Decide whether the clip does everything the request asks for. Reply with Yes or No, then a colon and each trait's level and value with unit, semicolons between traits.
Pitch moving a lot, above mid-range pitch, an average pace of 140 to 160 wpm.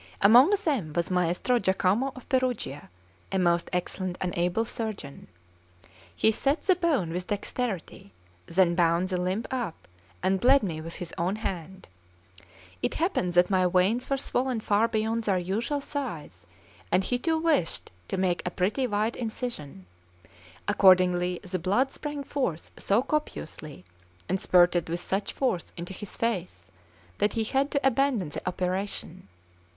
Yes: wide, 5.7 semitones; high, 195 Hz; average, 150 wpm